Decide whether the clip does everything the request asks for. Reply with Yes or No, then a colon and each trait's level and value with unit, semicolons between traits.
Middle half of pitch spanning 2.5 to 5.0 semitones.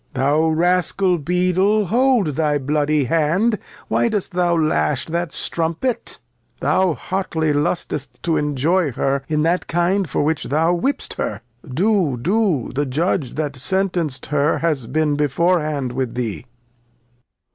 Yes: average, 4.0 semitones